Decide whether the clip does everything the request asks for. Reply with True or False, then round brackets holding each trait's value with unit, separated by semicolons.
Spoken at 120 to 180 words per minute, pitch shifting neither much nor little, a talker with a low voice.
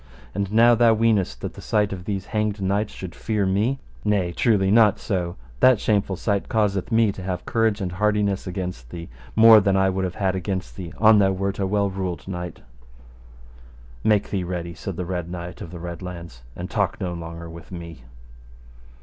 False (195 wpm; 3.0 semitones; 95 Hz)